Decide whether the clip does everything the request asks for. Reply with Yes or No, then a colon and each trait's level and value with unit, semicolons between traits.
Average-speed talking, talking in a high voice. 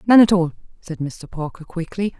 No: average, 190 wpm; medium, 180 Hz